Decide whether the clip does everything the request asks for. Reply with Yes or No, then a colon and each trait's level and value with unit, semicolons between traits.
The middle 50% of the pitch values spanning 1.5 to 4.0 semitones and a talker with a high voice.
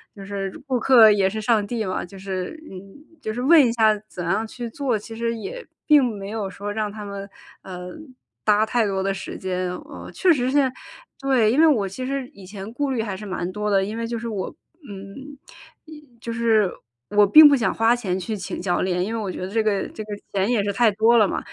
Yes: average, 3.5 semitones; high, 215 Hz